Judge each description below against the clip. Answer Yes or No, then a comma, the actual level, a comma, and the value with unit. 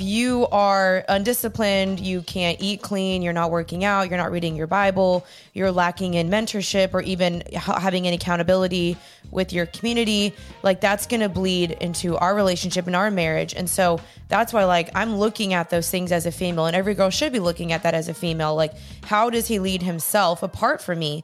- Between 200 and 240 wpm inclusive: Yes, fast, 205 wpm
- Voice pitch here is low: No, medium, 185 Hz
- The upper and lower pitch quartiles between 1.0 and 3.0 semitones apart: Yes, narrow, 2.5 semitones